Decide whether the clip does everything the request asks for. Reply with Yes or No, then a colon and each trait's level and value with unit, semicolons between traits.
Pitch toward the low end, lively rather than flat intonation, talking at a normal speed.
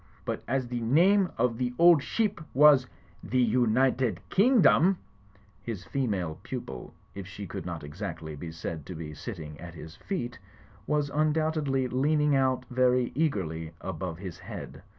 Yes: low, 125 Hz; wide, 8.4 semitones; average, 150 wpm